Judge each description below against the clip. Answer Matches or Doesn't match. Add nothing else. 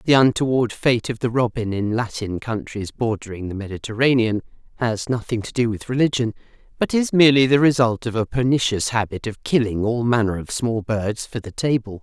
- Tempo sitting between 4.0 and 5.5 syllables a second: Matches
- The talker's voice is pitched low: Matches